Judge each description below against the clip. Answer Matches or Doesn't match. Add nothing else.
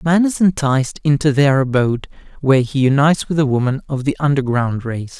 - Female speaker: Doesn't match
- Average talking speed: Matches